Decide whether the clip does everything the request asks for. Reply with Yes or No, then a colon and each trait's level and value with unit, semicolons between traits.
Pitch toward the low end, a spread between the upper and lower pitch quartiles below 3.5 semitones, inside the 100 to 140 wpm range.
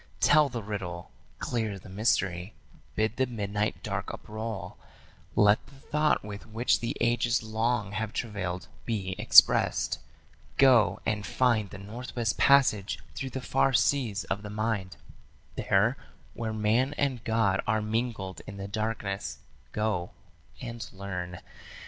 Yes: low, 110 Hz; average, 3.0 semitones; slow, 135 wpm